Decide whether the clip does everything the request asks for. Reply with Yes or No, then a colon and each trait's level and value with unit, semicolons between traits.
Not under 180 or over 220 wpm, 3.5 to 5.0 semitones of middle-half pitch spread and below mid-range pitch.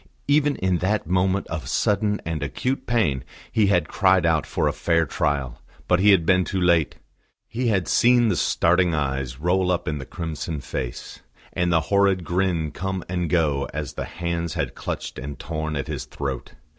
Yes: average, 185 wpm; average, 4.0 semitones; very low, 85 Hz